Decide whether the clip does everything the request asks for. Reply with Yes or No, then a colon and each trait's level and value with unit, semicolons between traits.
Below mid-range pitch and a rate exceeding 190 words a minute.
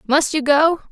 No: very high, 295 Hz; average, 200 wpm